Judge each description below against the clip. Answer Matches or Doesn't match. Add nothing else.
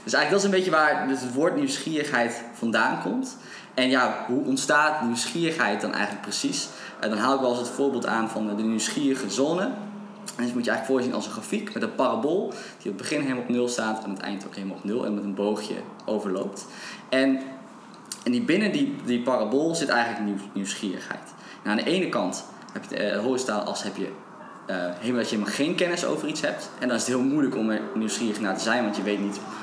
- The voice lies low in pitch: Matches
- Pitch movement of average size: Doesn't match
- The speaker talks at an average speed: Doesn't match